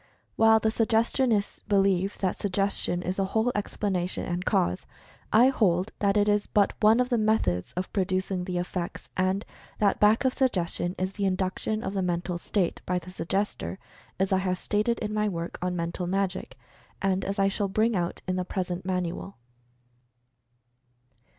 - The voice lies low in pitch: No, high, 195 Hz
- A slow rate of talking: No, average, 170 wpm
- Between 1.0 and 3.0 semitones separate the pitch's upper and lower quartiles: Yes, narrow, 2.5 semitones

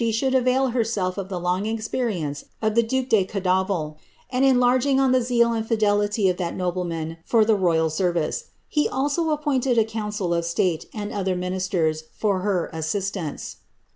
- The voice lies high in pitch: Yes, high, 205 Hz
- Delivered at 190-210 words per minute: No, average, 170 wpm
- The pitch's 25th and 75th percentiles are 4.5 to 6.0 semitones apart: Yes, average, 5.0 semitones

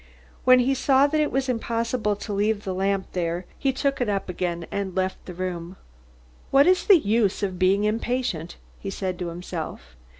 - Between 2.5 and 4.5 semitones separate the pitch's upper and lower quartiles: No, wide, 5.5 semitones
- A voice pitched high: Yes, high, 200 Hz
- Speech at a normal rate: Yes, average, 190 wpm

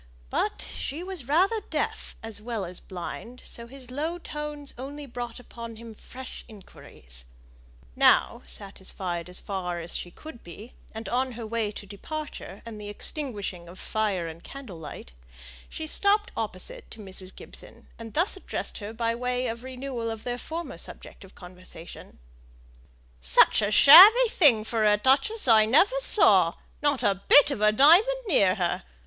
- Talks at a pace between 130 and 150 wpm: No, average, 165 wpm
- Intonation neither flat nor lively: No, wide, 6.4 semitones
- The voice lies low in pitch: No, high, 230 Hz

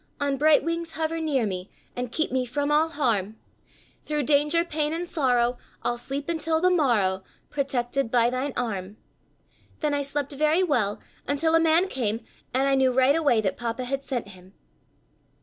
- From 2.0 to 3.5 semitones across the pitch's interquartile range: No, average, 4.4 semitones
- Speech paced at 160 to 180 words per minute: Yes, average, 175 wpm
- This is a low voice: No, very high, 275 Hz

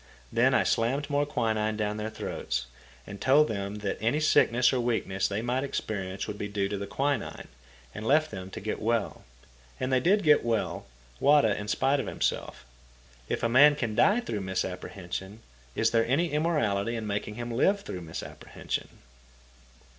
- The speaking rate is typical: Yes, average, 175 wpm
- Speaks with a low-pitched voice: Yes, low, 115 Hz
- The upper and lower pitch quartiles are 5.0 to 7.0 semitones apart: Yes, wide, 5.4 semitones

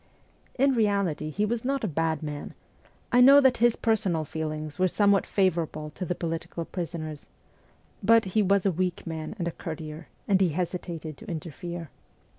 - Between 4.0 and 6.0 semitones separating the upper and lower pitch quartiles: Yes, average, 4.3 semitones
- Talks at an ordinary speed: Yes, average, 170 wpm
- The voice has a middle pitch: Yes, medium, 175 Hz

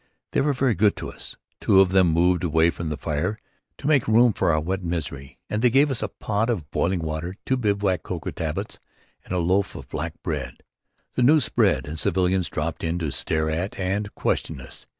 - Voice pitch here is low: Yes, very low, 90 Hz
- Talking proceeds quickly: Yes, fast, 210 wpm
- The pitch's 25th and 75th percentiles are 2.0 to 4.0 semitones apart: No, average, 4.6 semitones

